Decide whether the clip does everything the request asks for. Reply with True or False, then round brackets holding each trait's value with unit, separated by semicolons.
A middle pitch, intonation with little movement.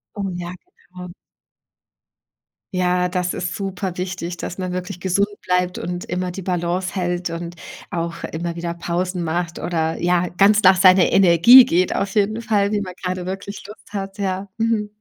True (180 Hz; 1.8 semitones)